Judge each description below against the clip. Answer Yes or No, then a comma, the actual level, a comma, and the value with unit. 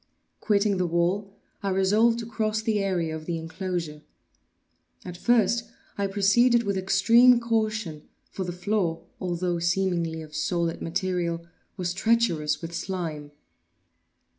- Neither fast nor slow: No, slow, 130 wpm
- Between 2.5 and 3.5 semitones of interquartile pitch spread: No, average, 4.1 semitones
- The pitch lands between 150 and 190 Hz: Yes, medium, 185 Hz